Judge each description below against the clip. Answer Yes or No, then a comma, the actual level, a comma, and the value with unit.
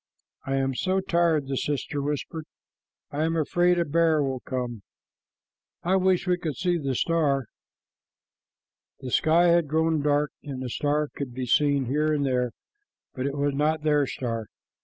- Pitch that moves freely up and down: No, average, 3.3 semitones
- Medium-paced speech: Yes, average, 165 wpm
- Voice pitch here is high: No, medium, 150 Hz